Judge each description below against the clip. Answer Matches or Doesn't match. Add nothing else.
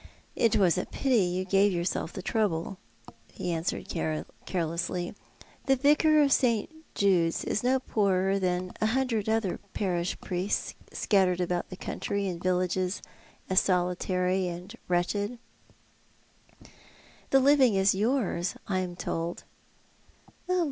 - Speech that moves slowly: Matches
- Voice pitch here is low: Doesn't match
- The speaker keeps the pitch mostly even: Doesn't match